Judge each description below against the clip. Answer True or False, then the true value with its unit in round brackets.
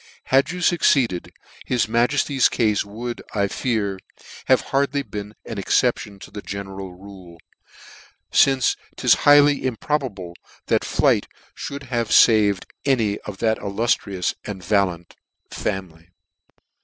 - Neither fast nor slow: False (120 wpm)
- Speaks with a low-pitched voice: True (110 Hz)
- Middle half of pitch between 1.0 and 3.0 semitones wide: False (4.9 semitones)